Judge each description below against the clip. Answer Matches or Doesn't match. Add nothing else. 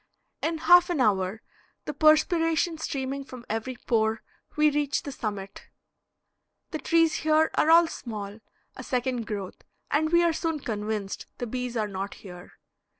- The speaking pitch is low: Doesn't match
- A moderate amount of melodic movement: Doesn't match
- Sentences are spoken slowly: Doesn't match